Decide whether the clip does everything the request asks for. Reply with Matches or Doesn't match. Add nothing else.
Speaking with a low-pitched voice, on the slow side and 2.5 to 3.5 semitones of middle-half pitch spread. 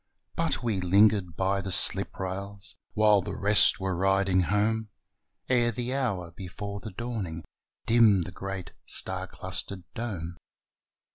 Matches